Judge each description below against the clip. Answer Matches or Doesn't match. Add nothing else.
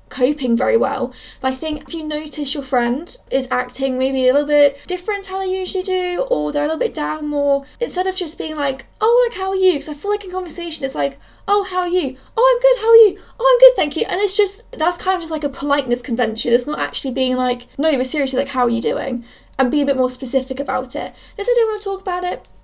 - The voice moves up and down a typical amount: Doesn't match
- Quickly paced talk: Matches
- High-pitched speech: Matches